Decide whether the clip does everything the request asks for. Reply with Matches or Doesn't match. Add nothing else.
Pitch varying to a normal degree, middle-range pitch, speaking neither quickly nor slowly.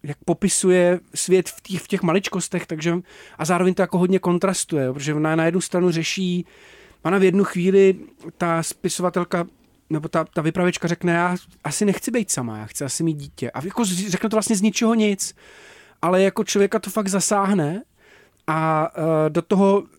Doesn't match